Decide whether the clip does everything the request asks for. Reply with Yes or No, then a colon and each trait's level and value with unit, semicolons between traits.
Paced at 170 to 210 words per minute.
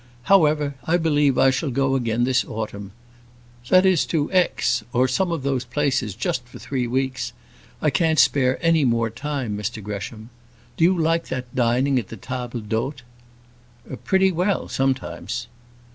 No: average, 160 wpm